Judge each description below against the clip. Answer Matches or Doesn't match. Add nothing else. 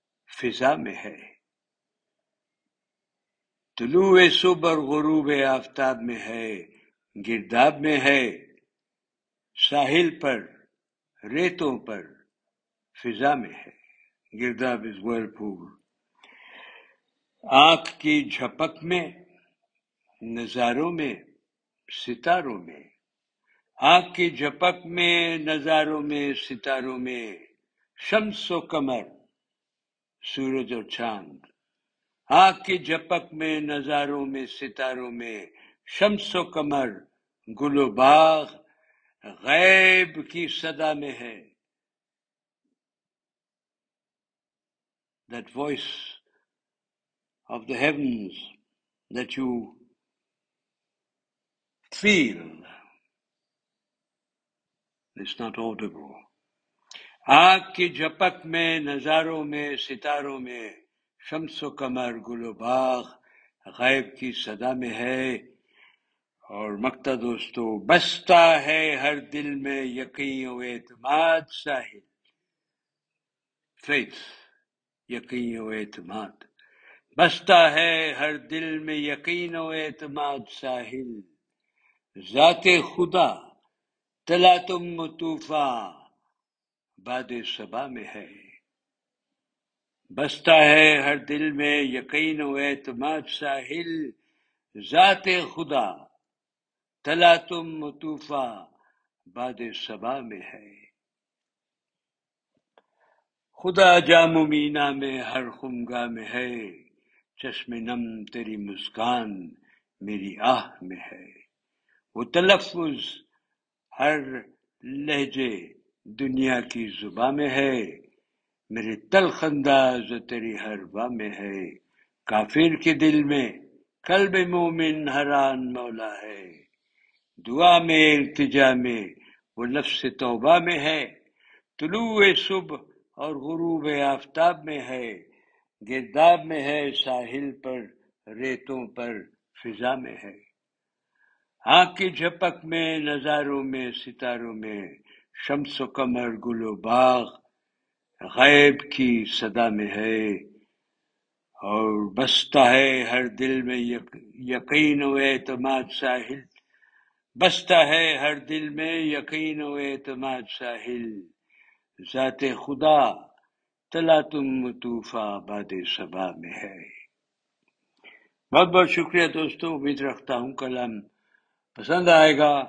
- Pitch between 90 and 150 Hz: Matches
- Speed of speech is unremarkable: Doesn't match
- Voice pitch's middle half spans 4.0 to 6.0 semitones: Matches